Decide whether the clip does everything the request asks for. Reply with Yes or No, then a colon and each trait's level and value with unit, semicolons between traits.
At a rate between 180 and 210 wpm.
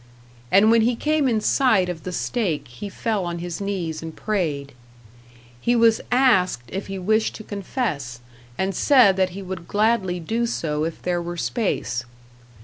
No: average, 170 wpm